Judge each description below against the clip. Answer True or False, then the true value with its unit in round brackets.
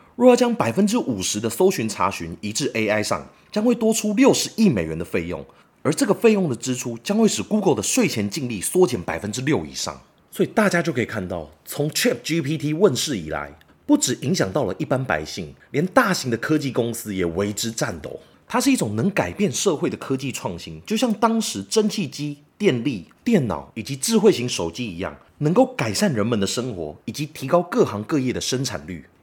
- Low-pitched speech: False (145 Hz)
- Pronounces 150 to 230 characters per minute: False (325 characters per minute)